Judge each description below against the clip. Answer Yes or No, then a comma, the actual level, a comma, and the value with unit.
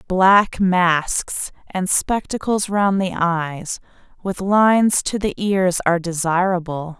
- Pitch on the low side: No, medium, 185 Hz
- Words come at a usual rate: No, slow, 120 wpm